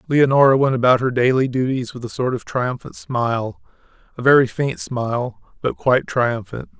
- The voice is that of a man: Yes, male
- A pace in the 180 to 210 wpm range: No, average, 160 wpm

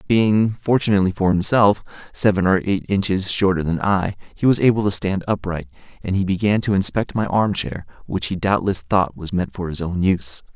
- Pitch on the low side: Yes, very low, 95 Hz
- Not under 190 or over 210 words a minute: Yes, average, 200 wpm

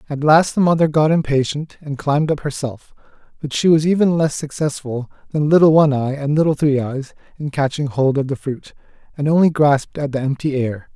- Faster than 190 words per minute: Yes, fast, 205 wpm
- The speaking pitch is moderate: Yes, medium, 145 Hz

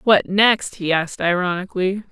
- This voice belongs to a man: No, female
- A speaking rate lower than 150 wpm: Yes, average, 140 wpm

